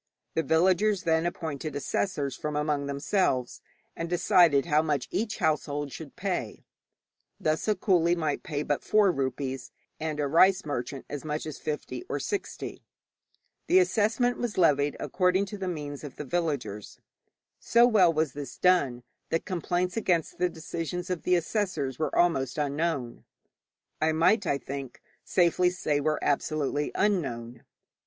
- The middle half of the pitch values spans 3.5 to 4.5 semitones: Yes, average, 4.1 semitones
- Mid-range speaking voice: Yes, medium, 160 Hz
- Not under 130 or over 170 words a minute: Yes, average, 150 wpm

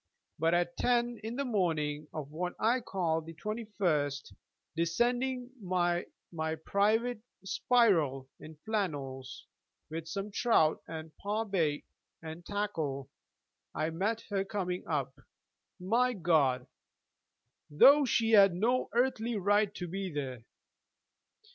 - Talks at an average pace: No, slow, 120 wpm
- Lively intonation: Yes, wide, 5.7 semitones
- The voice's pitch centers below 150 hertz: No, medium, 180 Hz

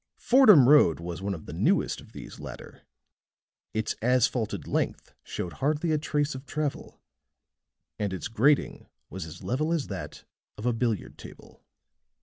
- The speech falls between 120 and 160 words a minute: Yes, average, 150 wpm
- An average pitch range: No, wide, 6.6 semitones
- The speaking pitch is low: Yes, low, 125 Hz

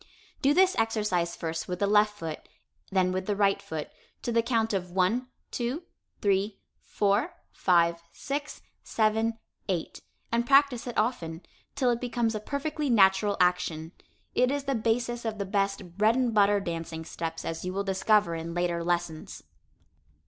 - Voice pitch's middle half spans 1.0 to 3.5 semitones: No, average, 4.9 semitones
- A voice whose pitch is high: Yes, high, 205 Hz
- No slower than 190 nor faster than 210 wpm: No, average, 165 wpm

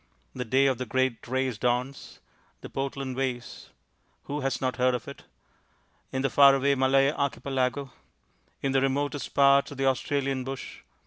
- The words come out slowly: No, average, 165 wpm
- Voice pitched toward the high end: No, low, 135 Hz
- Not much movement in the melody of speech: Yes, narrow, 1.2 semitones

